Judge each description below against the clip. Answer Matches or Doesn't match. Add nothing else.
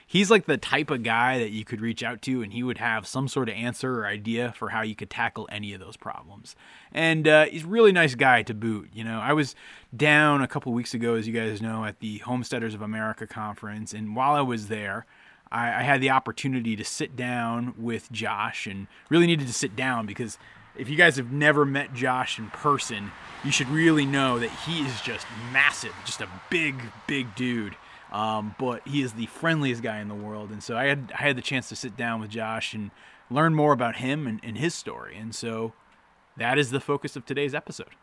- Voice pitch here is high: Doesn't match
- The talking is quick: Matches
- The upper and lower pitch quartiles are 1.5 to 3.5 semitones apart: Doesn't match